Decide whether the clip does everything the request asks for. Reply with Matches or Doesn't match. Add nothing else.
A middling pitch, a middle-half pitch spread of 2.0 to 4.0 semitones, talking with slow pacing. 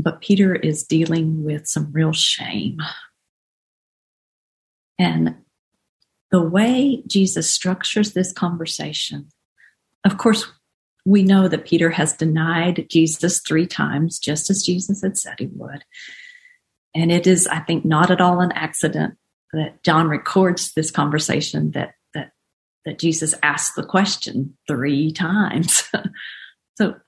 Matches